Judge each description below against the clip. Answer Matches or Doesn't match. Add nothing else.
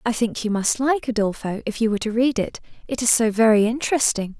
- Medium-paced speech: Doesn't match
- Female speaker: Matches